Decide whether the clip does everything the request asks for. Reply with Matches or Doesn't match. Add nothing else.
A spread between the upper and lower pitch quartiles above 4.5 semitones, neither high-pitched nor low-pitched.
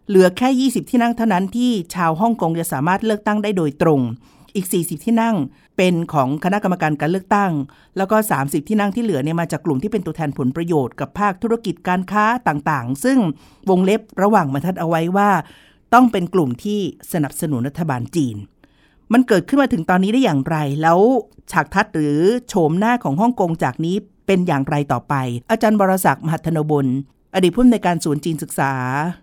Matches